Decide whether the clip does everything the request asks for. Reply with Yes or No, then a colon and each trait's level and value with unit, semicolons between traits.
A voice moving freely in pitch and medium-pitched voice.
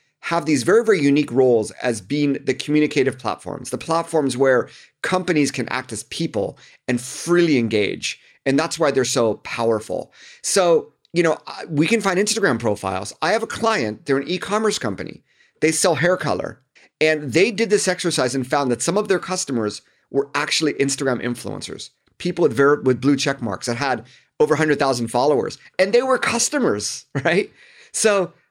Yes: wide, 6.4 semitones; medium, 145 Hz